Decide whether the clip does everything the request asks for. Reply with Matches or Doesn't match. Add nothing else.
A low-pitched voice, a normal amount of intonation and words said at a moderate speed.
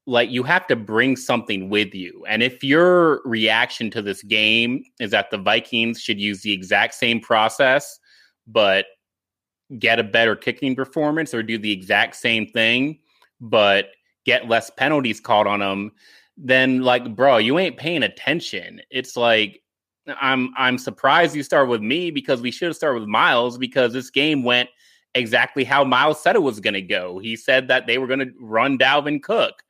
Matches